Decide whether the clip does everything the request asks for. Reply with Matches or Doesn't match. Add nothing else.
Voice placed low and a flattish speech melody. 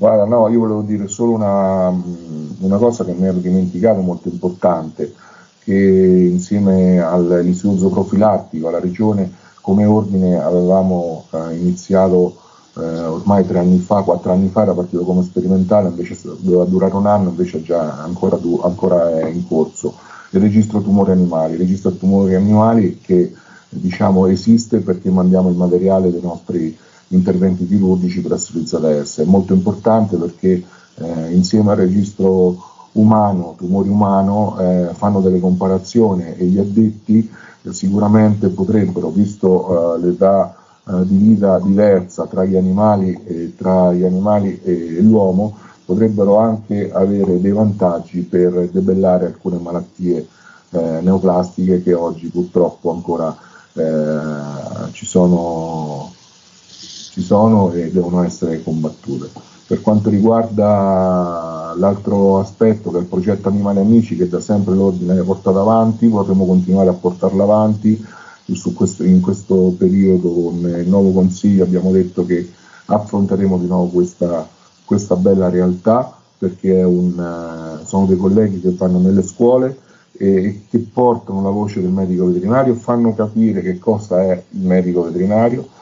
Matches